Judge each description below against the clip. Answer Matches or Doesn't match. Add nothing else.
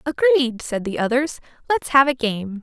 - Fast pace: Doesn't match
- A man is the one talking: Doesn't match